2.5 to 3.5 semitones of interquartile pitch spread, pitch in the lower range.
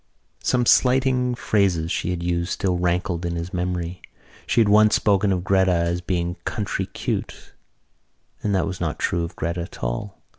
Yes: average, 2.9 semitones; very low, 90 Hz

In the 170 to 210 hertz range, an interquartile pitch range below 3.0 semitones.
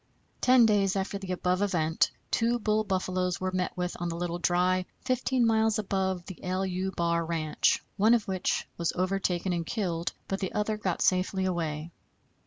Yes: medium, 185 Hz; narrow, 2.6 semitones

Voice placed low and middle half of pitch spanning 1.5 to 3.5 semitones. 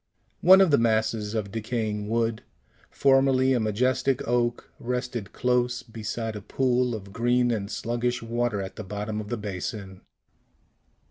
Yes: low, 115 Hz; narrow, 2.6 semitones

